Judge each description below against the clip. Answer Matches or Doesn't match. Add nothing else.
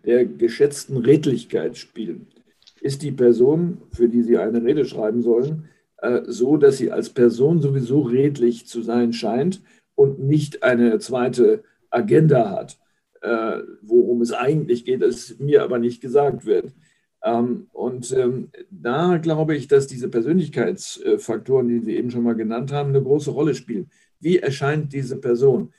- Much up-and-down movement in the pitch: Matches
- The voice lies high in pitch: Doesn't match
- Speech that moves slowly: Doesn't match